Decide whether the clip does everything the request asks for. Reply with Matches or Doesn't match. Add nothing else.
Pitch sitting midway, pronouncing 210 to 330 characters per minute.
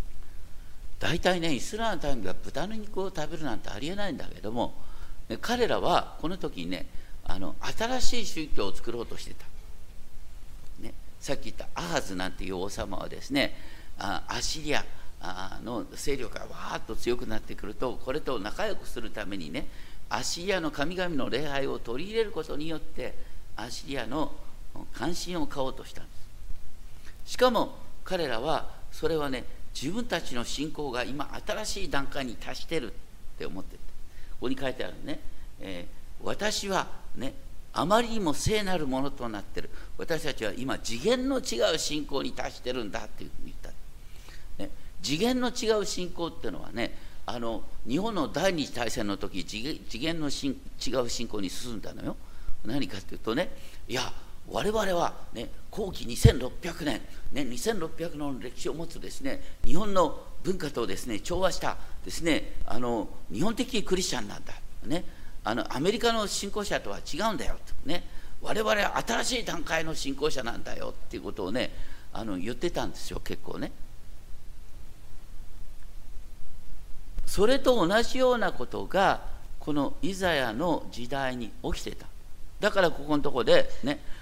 Matches